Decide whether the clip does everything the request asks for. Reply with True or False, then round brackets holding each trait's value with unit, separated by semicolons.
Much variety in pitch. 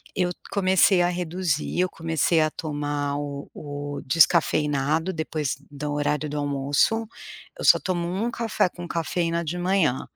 False (3.4 semitones)